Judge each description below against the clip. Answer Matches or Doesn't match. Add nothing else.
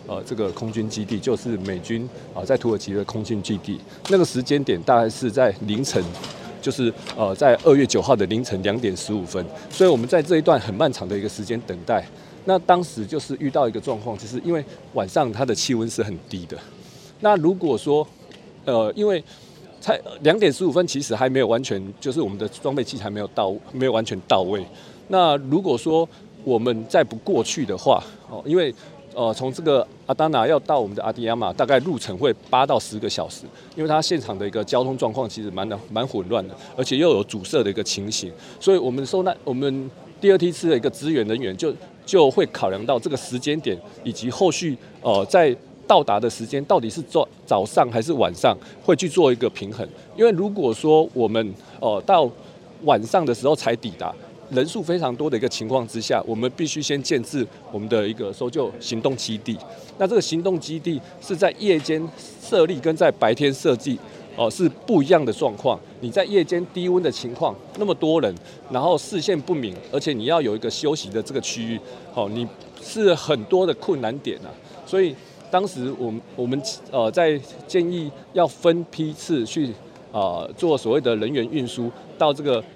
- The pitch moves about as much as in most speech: Doesn't match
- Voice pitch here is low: Matches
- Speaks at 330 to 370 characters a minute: Doesn't match